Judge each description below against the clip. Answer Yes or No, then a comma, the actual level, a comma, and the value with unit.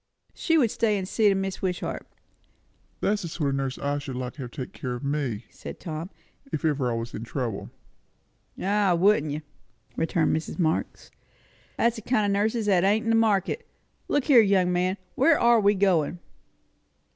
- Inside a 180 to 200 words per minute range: Yes, average, 190 wpm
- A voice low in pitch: No, medium, 185 Hz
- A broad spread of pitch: Yes, wide, 6.5 semitones